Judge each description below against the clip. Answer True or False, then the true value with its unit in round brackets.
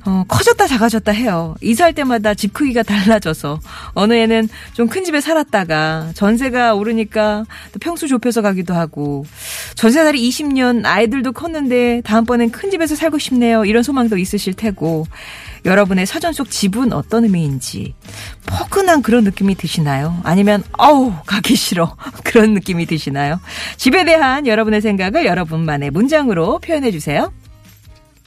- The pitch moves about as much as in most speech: False (6.4 semitones)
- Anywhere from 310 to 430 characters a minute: True (340 characters per minute)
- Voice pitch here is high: True (220 Hz)